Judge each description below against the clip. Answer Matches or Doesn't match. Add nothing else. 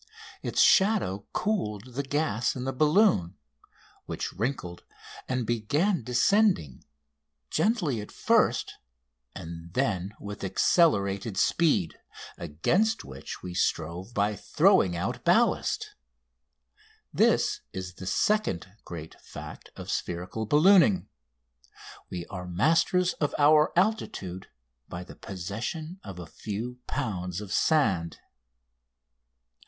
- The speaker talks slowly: Matches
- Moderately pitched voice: Doesn't match